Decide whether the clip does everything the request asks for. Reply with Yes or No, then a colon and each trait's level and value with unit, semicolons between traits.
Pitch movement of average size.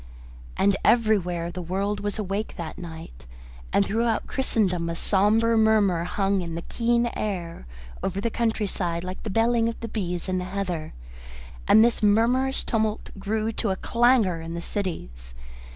Yes: average, 4.1 semitones